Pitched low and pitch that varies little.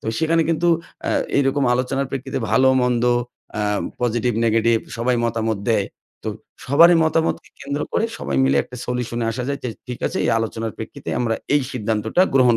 No: low, 125 Hz; average, 3.5 semitones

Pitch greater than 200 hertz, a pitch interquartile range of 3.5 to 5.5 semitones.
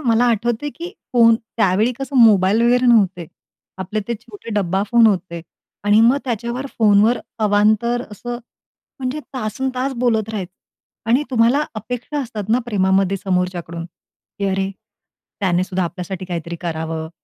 Yes: high, 215 Hz; average, 4.2 semitones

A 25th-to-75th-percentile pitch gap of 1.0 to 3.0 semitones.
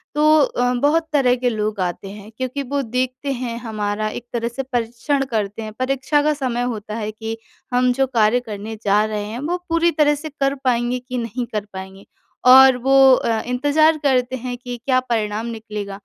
No: average, 3.6 semitones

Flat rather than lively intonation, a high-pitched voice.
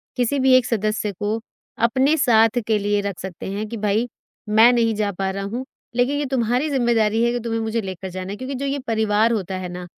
No: average, 3.0 semitones; high, 225 Hz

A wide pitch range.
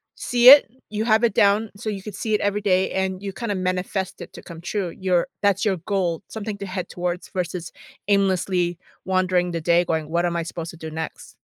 No: average, 2.7 semitones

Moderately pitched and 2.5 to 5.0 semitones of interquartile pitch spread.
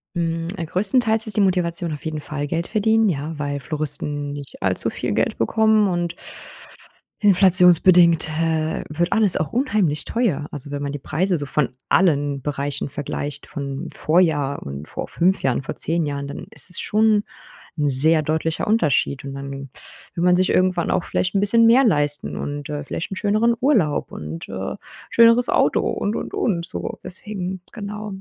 No: medium, 165 Hz; wide, 5.5 semitones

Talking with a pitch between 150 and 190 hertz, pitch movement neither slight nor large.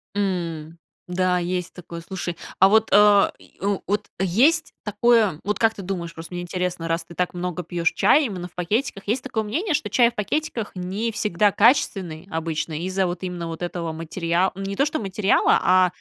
Yes: medium, 185 Hz; average, 3.4 semitones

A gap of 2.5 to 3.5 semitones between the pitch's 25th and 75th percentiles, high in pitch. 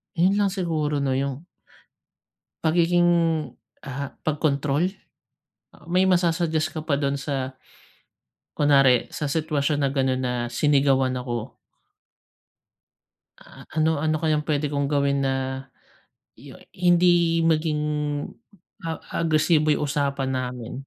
No: average, 2.9 semitones; medium, 150 Hz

